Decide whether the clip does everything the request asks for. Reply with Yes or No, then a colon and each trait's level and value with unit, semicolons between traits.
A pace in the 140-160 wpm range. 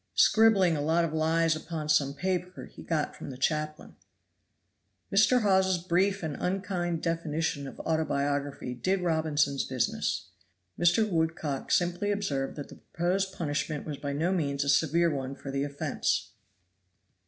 Yes: average, 145 wpm